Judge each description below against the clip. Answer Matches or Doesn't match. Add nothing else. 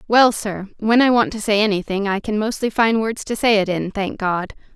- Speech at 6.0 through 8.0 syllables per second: Doesn't match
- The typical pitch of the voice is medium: Doesn't match